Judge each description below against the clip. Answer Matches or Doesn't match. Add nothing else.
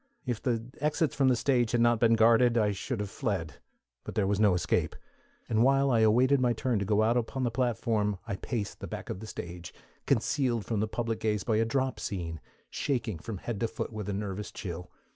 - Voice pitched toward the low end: Matches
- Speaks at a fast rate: Matches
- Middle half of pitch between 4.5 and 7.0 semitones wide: Doesn't match